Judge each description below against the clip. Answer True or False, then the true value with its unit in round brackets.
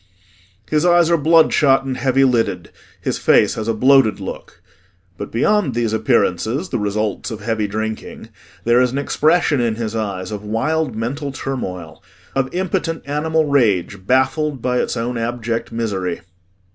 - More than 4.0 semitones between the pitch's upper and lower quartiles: True (4.6 semitones)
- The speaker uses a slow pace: False (155 wpm)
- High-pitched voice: False (120 Hz)